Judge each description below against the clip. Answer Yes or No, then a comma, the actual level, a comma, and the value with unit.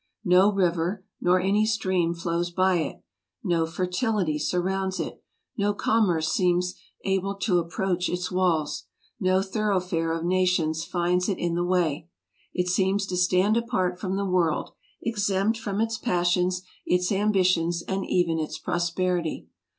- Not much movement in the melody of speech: Yes, narrow, 1.9 semitones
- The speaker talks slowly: No, average, 145 wpm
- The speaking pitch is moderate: Yes, medium, 180 Hz